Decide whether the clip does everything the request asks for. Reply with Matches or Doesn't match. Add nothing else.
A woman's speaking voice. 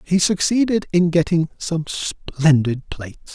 Doesn't match